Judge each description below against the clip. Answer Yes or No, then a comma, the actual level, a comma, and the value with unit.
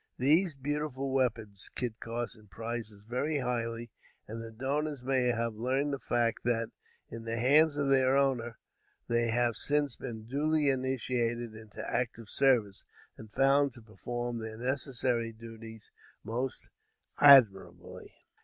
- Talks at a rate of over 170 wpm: No, slow, 135 wpm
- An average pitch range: Yes, average, 3.0 semitones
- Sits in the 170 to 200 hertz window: No, low, 120 Hz